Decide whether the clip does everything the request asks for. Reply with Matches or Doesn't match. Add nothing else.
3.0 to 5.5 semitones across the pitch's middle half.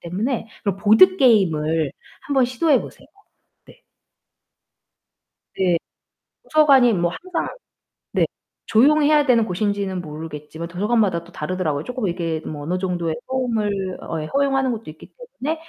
Doesn't match